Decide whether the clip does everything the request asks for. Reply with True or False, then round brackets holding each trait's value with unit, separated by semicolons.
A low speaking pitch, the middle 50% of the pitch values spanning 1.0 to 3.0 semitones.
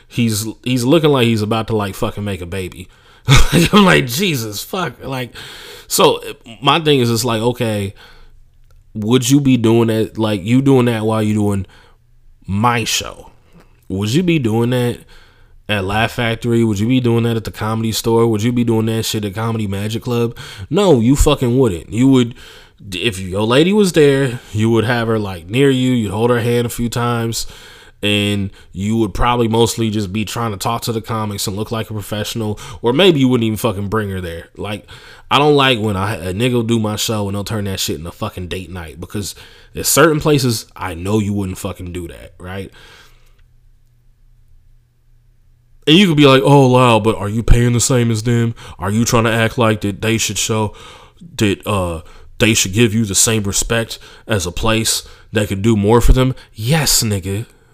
True (115 Hz; 2.7 semitones)